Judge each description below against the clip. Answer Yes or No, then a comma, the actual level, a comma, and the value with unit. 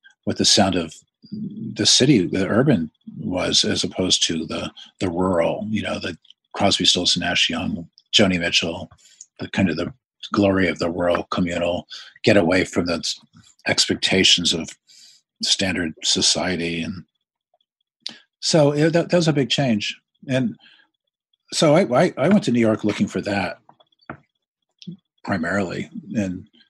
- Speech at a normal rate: Yes, average, 145 wpm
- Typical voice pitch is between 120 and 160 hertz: No, low, 105 Hz